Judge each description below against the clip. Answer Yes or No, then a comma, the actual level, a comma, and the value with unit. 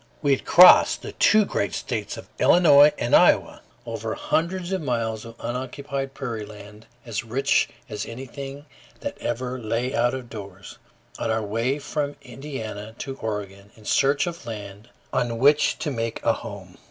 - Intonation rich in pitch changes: No, average, 4.2 semitones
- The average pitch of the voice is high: No, low, 125 Hz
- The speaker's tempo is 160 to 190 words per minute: Yes, average, 165 wpm